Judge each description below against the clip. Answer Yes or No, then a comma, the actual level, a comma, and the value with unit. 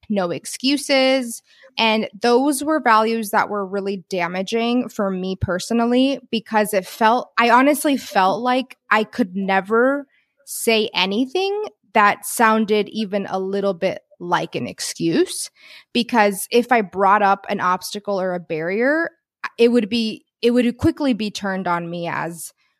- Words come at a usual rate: Yes, average, 145 wpm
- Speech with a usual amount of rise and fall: Yes, average, 4.4 semitones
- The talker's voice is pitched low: No, high, 220 Hz